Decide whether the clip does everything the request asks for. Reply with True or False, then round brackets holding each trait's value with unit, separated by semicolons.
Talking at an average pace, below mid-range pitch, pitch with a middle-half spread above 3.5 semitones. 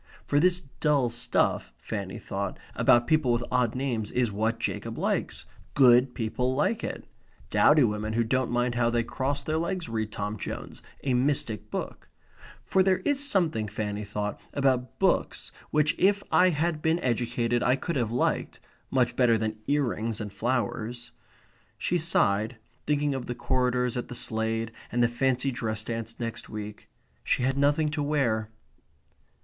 True (165 wpm; 125 Hz; 4.2 semitones)